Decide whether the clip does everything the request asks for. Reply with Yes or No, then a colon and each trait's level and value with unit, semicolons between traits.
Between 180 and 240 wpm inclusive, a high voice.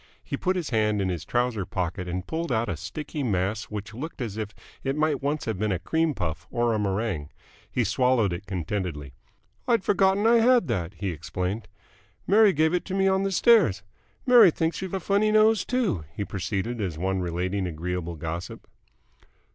No: average, 190 wpm; low, 110 Hz